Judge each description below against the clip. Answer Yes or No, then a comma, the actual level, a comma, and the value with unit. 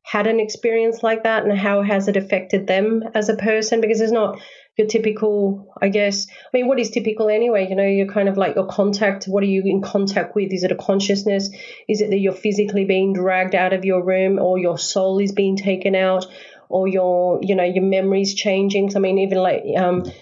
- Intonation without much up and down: Yes, narrow, 1.9 semitones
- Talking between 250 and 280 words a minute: No, fast, 225 wpm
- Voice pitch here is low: No, high, 195 Hz